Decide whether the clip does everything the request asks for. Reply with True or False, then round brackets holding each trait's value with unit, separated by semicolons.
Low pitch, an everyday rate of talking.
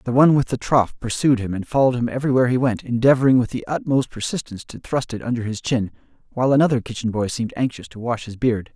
False (125 Hz; 235 wpm)